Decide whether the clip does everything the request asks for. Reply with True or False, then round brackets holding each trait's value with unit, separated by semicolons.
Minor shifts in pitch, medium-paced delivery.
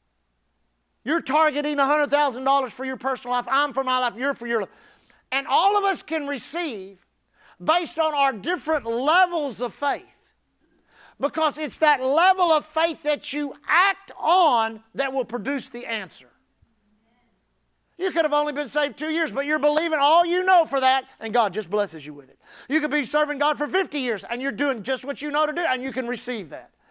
False (4.2 semitones; 195 wpm)